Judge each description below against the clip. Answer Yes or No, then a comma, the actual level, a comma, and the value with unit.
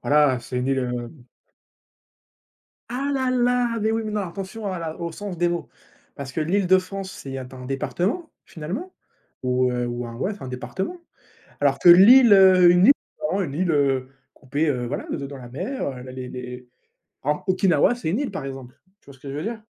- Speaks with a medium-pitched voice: Yes, medium, 160 Hz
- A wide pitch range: Yes, wide, 7.4 semitones